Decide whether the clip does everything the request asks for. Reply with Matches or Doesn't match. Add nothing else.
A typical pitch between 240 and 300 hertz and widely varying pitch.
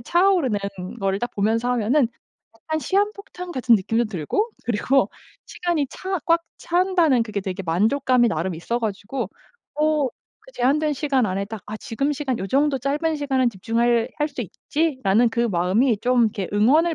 Matches